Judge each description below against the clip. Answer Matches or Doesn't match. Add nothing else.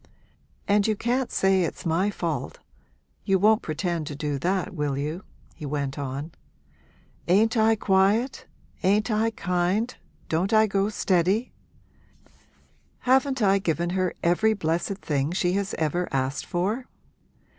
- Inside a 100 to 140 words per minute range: Matches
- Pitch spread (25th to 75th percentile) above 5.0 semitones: Doesn't match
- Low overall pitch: Doesn't match